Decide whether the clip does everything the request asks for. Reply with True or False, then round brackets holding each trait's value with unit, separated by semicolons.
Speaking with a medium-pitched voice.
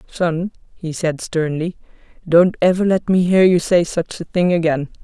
True (170 Hz)